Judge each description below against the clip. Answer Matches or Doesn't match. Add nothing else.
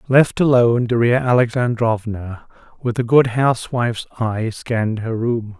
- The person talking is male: Matches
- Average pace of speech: Doesn't match